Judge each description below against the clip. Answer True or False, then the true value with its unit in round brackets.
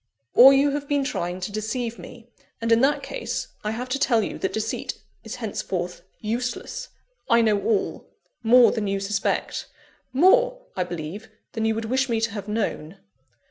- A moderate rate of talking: True (180 wpm)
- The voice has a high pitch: True (225 Hz)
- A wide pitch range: False (3.8 semitones)